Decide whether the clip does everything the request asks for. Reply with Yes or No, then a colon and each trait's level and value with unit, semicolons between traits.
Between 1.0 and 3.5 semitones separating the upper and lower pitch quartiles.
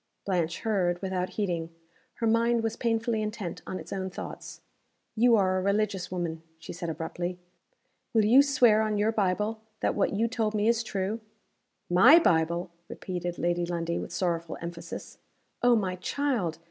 No: average, 4.2 semitones